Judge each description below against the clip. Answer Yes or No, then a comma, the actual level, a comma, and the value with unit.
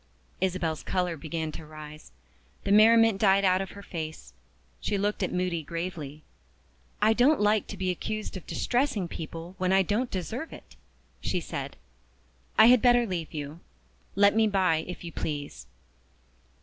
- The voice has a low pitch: No, medium, 185 Hz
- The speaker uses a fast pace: No, average, 160 wpm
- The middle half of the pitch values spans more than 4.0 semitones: Yes, average, 4.4 semitones